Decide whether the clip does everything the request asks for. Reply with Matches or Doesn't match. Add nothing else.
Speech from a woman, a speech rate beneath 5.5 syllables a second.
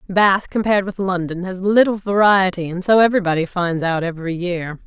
Doesn't match